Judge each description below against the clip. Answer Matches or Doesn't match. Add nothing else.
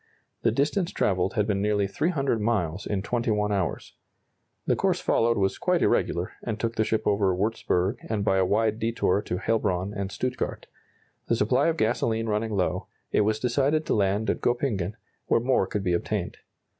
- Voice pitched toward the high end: Doesn't match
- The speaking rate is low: Doesn't match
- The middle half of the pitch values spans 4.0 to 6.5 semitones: Doesn't match